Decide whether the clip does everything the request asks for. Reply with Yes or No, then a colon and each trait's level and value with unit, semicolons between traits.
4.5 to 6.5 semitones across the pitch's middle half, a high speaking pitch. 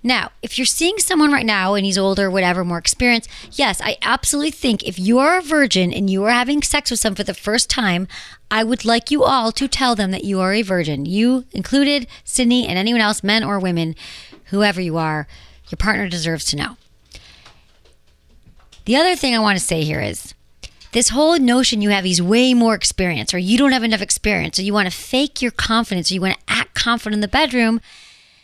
Yes: average, 5.0 semitones; high, 215 Hz